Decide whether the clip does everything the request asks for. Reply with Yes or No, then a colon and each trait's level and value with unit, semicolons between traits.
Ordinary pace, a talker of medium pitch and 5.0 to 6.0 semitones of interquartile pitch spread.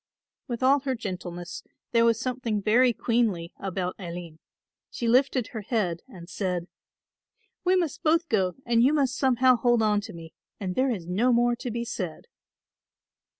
No: average, 165 wpm; high, 230 Hz; wide, 5.5 semitones